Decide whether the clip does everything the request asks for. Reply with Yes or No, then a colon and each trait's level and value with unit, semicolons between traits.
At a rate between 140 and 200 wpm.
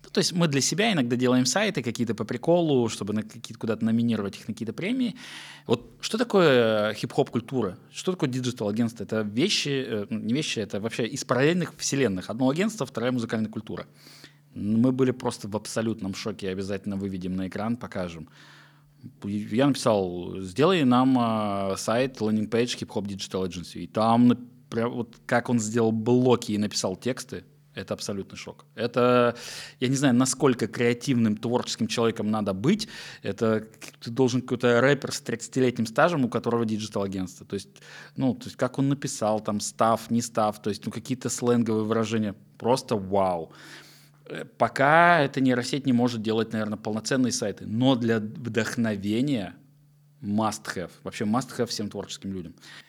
Yes: fast, 160 wpm